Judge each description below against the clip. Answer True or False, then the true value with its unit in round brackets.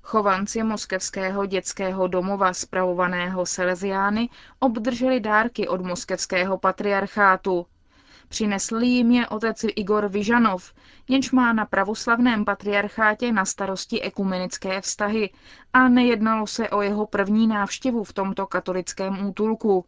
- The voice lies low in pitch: False (200 Hz)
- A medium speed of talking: False (110 wpm)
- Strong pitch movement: False (2.8 semitones)